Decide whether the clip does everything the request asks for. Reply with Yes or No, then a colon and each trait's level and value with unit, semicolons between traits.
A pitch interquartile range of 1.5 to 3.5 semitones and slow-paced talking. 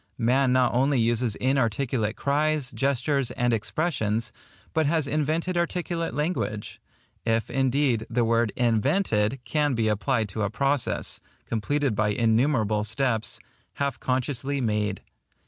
No: average, 4.1 semitones; slow, 125 wpm